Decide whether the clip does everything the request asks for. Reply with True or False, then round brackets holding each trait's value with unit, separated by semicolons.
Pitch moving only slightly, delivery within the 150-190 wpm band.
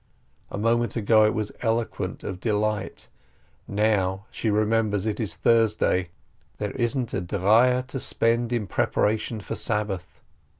False (2.2 semitones; 140 wpm)